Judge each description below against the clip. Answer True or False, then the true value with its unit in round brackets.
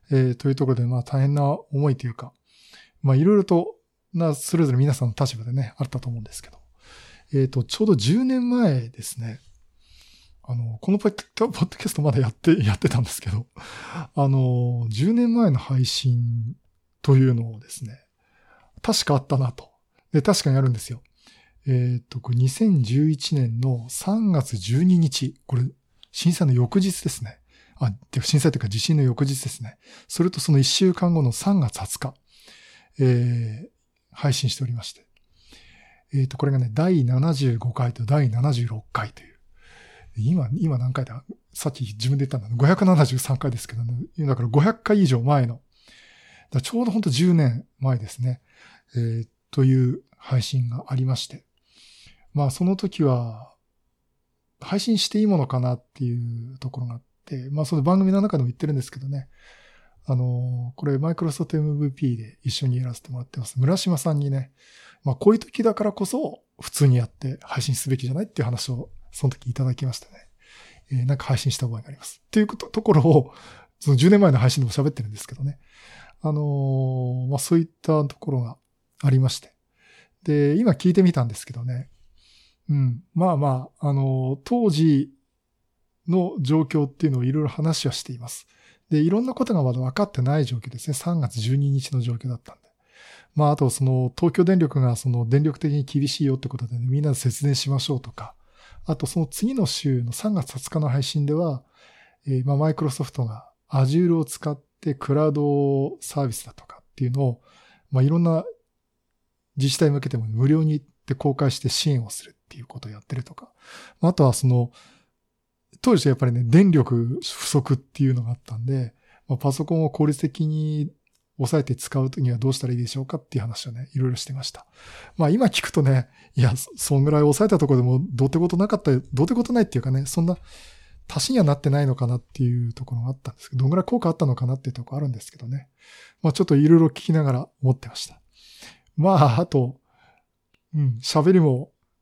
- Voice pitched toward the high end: False (135 Hz)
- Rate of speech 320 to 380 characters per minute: True (360 characters per minute)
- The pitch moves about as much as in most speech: True (3.8 semitones)